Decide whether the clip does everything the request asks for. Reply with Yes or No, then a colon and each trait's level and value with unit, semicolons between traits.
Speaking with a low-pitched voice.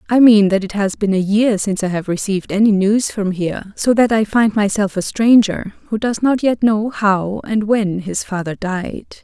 No: high, 205 Hz